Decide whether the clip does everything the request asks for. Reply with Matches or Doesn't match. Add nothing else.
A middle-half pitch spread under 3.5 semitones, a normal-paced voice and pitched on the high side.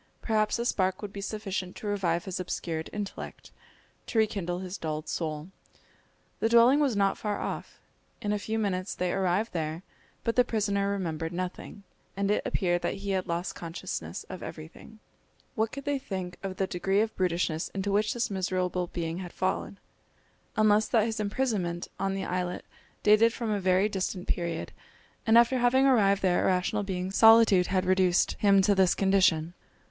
Matches